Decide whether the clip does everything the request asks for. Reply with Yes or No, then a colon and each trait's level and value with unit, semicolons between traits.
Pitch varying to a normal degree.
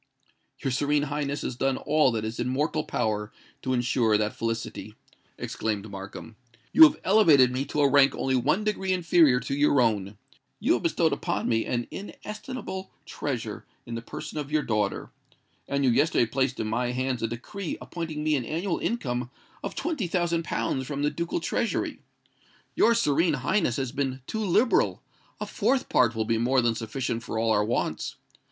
No: wide, 5.8 semitones